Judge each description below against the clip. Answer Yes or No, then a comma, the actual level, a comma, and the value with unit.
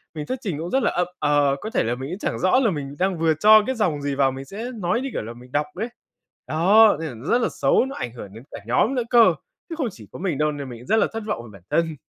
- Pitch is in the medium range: Yes, medium, 165 Hz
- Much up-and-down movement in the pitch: Yes, wide, 8.0 semitones